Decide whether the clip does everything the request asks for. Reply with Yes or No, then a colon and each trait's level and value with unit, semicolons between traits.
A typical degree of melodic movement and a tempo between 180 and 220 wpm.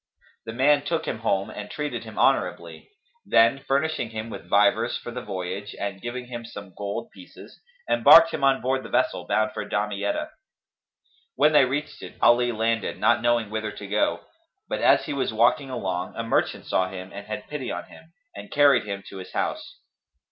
Yes: average, 4.6 semitones; average, 190 wpm